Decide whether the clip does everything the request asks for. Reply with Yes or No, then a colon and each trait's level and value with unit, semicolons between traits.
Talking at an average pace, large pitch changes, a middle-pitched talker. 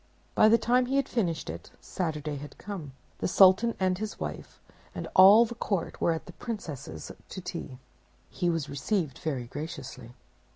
Yes: average, 170 wpm; wide, 6.3 semitones; medium, 175 Hz